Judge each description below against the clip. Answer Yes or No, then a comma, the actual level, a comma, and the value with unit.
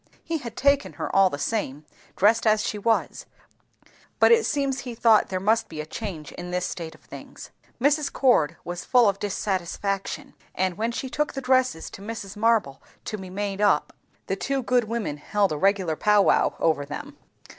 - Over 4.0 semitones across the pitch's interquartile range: Yes, average, 4.6 semitones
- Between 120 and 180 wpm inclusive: No, average, 190 wpm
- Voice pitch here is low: No, high, 210 Hz